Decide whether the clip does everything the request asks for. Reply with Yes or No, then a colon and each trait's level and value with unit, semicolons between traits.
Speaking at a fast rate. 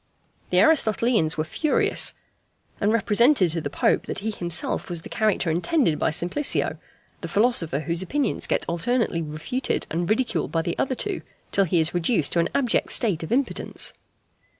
No: average, 170 wpm